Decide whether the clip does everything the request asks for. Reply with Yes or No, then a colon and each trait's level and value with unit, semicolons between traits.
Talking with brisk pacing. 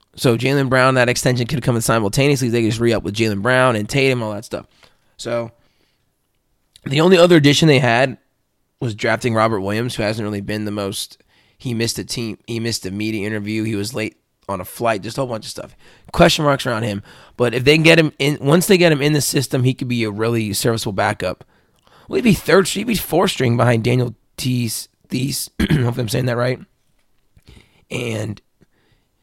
Yes: fast, 215 wpm